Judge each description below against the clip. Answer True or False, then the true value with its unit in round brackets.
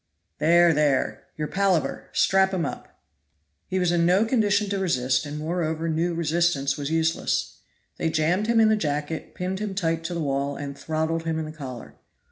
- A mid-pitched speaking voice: True (165 Hz)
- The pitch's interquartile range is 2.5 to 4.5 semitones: True (3.3 semitones)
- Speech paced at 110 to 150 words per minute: False (185 wpm)